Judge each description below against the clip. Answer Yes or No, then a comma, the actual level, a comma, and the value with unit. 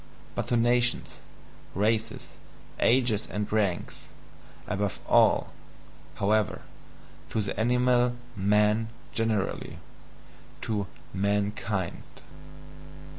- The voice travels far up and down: No, narrow, 2.4 semitones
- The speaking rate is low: Yes, slow, 75 wpm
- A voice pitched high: No, low, 110 Hz